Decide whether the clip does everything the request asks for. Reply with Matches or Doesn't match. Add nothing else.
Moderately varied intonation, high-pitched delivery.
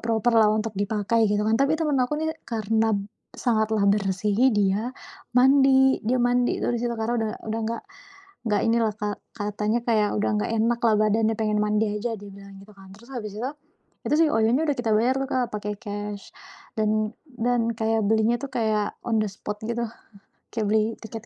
Doesn't match